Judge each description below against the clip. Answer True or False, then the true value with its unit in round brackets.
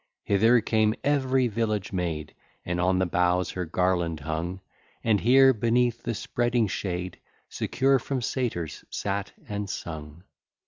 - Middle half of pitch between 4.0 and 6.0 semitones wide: True (5.1 semitones)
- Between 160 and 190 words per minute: False (135 wpm)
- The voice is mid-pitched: False (100 Hz)